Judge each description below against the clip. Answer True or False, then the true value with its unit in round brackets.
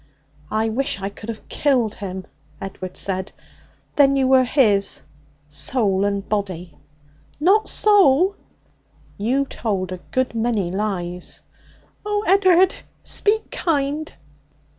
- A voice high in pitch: True (225 Hz)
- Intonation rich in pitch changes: True (6.7 semitones)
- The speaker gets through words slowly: True (115 wpm)